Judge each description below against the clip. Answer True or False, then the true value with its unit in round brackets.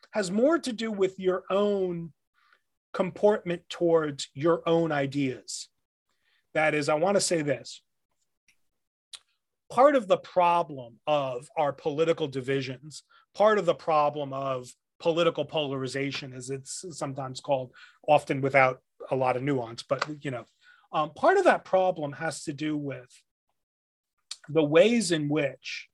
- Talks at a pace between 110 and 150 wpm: True (140 wpm)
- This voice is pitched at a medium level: True (155 Hz)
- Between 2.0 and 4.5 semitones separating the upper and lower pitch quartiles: False (5.0 semitones)